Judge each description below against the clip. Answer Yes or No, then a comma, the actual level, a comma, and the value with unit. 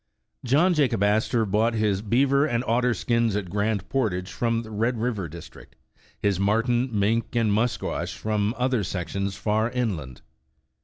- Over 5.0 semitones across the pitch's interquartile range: No, average, 3.0 semitones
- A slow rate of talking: No, average, 155 wpm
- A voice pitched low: Yes, low, 110 Hz